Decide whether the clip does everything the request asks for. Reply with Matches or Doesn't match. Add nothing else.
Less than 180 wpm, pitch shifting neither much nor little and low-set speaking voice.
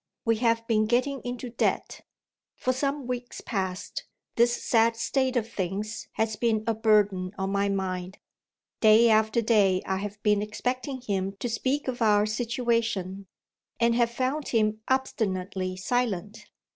Doesn't match